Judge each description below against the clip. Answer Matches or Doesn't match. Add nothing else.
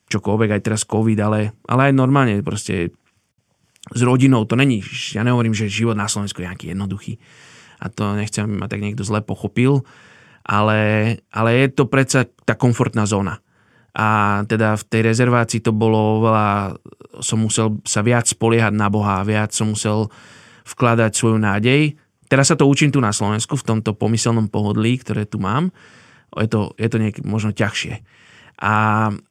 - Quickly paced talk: Matches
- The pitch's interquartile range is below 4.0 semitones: Matches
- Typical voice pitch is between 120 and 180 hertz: Doesn't match